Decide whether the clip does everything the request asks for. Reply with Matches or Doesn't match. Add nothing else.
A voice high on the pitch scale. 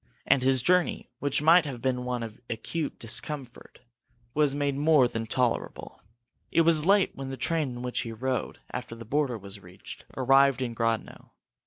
Doesn't match